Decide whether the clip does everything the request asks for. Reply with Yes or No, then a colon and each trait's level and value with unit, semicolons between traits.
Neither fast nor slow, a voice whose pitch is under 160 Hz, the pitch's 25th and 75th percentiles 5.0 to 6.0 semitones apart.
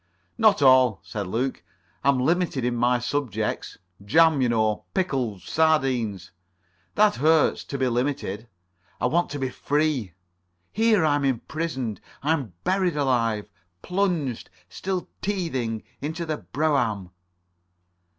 No: slow, 120 wpm; low, 135 Hz; wide, 5.5 semitones